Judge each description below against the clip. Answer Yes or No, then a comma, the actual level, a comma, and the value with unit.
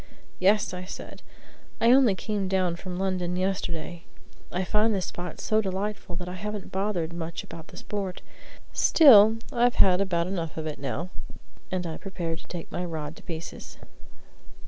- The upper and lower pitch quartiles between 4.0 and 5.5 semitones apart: No, average, 3.0 semitones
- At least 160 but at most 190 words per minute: Yes, average, 170 wpm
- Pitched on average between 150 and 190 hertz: Yes, medium, 185 Hz